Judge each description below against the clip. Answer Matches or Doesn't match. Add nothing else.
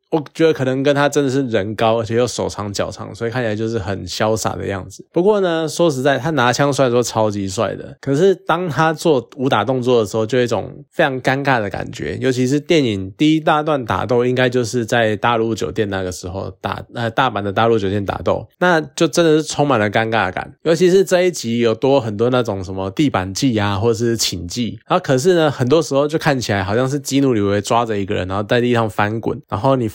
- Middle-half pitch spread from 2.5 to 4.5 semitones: Doesn't match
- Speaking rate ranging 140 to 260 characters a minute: Doesn't match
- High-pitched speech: Doesn't match